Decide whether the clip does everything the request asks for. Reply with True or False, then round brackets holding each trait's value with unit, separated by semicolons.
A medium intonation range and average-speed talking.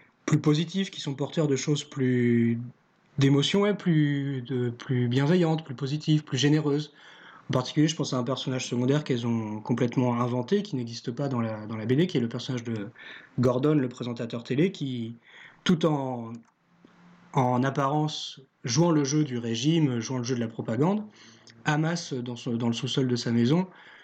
True (3.7 semitones; 175 wpm)